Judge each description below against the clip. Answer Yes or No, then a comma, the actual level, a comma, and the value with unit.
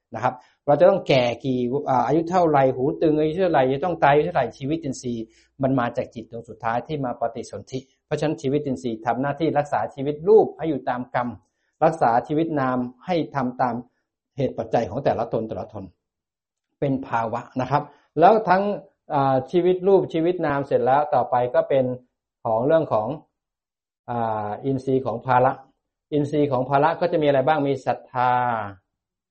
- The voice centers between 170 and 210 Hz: No, low, 135 Hz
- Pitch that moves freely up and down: No, average, 3.9 semitones